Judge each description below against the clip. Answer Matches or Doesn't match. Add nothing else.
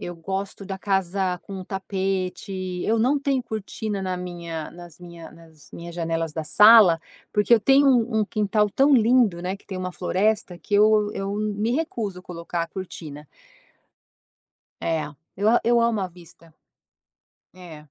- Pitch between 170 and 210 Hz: Matches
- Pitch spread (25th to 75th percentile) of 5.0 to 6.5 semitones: Doesn't match